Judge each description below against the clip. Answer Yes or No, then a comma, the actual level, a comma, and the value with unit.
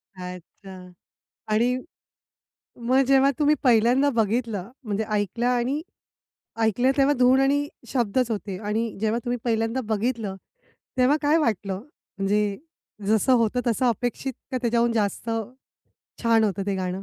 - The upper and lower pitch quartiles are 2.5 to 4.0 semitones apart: Yes, average, 3.5 semitones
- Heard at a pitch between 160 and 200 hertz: No, high, 230 Hz